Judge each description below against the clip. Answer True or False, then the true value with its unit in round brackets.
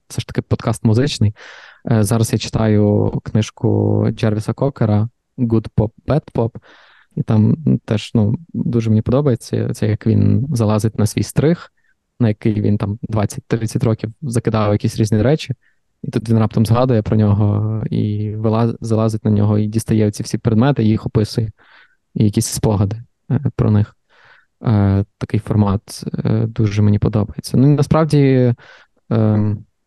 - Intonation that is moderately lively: False (2.3 semitones)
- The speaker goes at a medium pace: True (145 wpm)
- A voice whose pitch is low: True (110 Hz)